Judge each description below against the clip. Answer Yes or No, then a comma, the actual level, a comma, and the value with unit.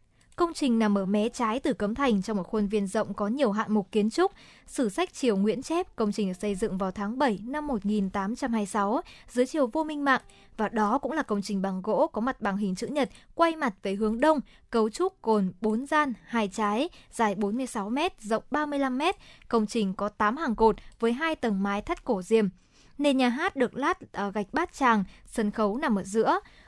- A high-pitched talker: Yes, high, 225 Hz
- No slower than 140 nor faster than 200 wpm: No, average, 220 wpm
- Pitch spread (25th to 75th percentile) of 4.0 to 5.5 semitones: Yes, average, 4.8 semitones